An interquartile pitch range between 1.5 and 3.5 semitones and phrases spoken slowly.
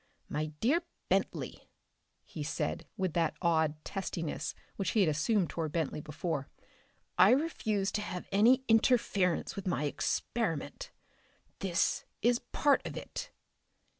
No: wide, 5.6 semitones; slow, 130 wpm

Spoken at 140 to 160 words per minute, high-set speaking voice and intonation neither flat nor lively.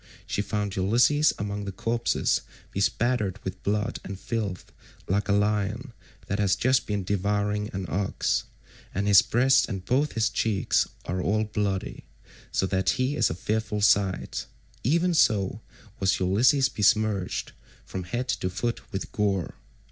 No: average, 150 wpm; low, 105 Hz; average, 3.1 semitones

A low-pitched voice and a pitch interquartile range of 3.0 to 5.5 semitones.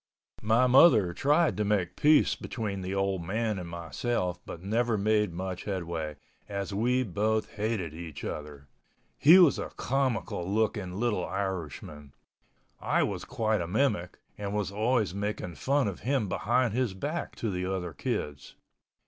Yes: low, 100 Hz; average, 4.4 semitones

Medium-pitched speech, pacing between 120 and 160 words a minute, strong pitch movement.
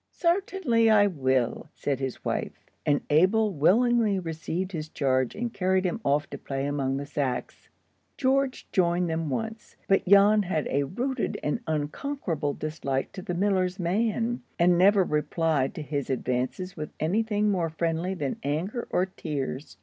Yes: medium, 175 Hz; average, 155 wpm; wide, 6.0 semitones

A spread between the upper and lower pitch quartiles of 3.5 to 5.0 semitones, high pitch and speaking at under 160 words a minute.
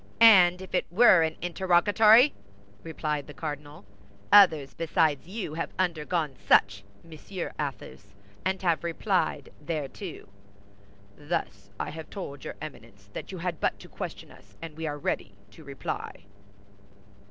No: average, 4.0 semitones; medium, 160 Hz; average, 140 wpm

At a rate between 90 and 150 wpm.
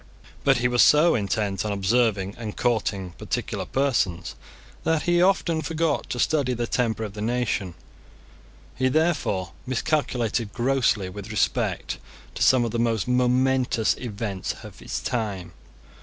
Yes: average, 140 wpm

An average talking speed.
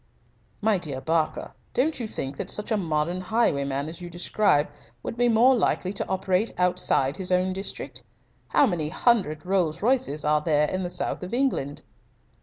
Yes: average, 175 wpm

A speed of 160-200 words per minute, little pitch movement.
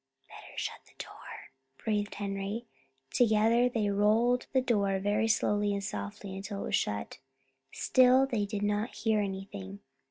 No: average, 150 wpm; narrow, 2.2 semitones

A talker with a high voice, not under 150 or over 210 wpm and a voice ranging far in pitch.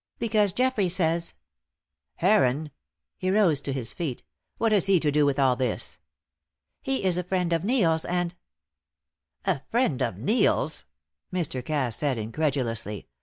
No: medium, 160 Hz; average, 155 wpm; wide, 6.3 semitones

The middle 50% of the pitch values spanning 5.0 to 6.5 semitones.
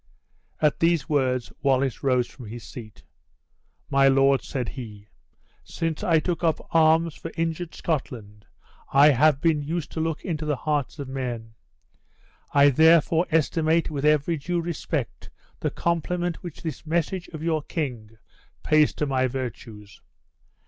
No: average, 4.0 semitones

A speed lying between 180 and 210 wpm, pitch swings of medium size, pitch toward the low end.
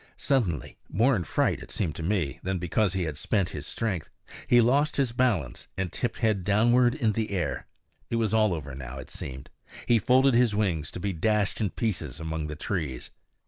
No: average, 200 wpm; wide, 6.3 semitones; low, 100 Hz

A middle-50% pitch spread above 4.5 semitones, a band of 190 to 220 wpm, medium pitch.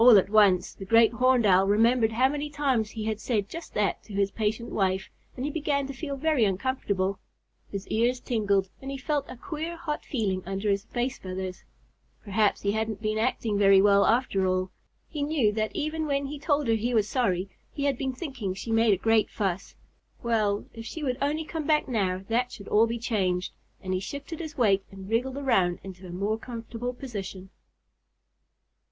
No: average, 5.1 semitones; average, 200 wpm; high, 225 Hz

